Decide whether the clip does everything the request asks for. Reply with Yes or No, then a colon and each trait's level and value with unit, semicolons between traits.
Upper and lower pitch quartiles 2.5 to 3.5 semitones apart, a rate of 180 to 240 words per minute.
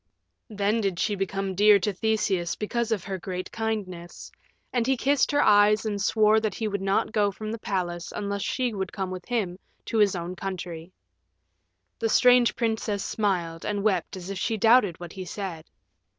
Yes: average, 2.9 semitones; average, 185 wpm